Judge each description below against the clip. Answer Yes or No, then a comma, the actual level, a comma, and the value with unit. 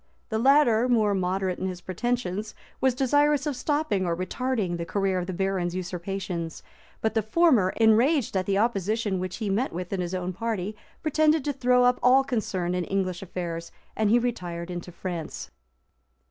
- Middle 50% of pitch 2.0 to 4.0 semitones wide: No, average, 5.3 semitones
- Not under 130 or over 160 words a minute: No, average, 175 wpm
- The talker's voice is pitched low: No, high, 200 Hz